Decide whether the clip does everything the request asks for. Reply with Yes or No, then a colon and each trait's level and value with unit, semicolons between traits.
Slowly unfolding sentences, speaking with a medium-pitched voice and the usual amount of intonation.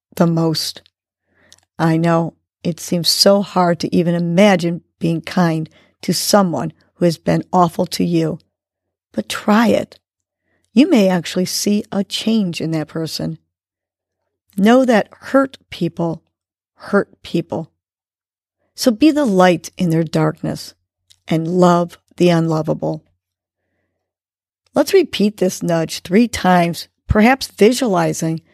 Yes: slow, 120 wpm; medium, 170 Hz; average, 4.7 semitones